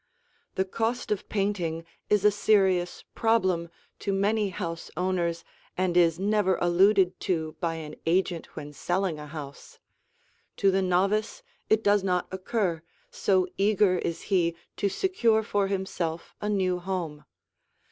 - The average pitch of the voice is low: No, medium, 185 Hz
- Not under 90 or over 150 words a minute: Yes, average, 140 wpm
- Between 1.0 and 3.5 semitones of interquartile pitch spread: Yes, average, 3.1 semitones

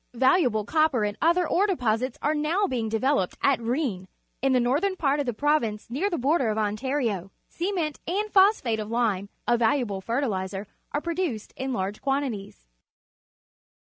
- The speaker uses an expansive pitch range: Yes, wide, 6.1 semitones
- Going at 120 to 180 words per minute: Yes, average, 170 wpm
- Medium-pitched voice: No, very high, 255 Hz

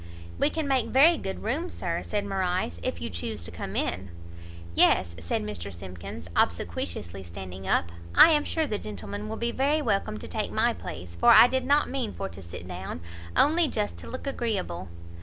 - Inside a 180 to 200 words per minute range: Yes, average, 195 wpm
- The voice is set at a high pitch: No, low, 105 Hz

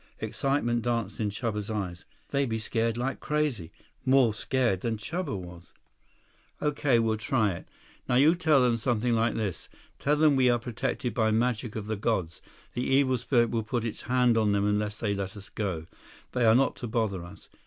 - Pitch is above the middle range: No, low, 115 Hz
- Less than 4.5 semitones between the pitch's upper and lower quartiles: Yes, average, 3.3 semitones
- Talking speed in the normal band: Yes, average, 190 wpm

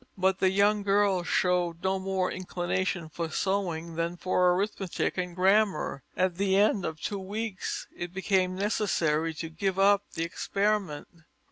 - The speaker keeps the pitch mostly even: Yes, narrow, 2.3 semitones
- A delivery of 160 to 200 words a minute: No, average, 150 wpm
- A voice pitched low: No, medium, 185 Hz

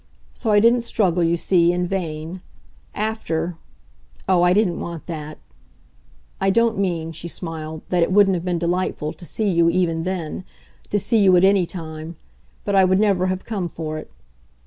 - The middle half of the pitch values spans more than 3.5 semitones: No, average, 2.7 semitones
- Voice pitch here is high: No, medium, 180 Hz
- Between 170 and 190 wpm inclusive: Yes, average, 180 wpm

